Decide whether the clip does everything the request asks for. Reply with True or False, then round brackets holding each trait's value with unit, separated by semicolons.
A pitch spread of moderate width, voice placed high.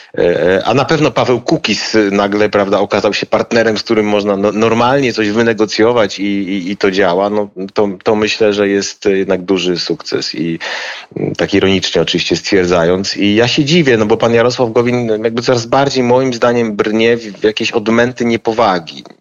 False (3.2 semitones; 115 Hz)